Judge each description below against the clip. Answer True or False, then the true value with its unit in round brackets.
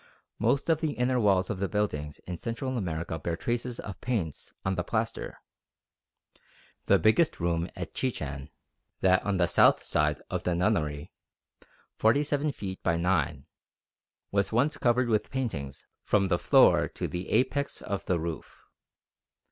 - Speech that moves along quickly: False (150 wpm)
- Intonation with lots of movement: True (6.0 semitones)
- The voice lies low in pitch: True (95 Hz)